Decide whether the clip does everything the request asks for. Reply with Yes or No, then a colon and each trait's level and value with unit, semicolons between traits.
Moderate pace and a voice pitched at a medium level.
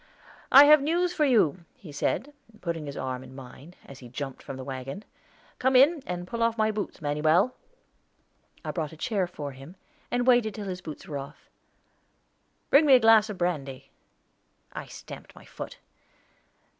Yes: average, 180 wpm; medium, 180 Hz